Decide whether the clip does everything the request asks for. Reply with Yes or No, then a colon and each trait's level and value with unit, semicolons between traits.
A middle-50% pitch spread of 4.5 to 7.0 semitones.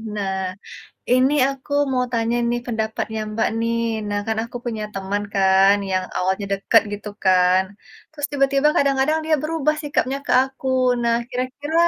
Yes: average, 5.2 semitones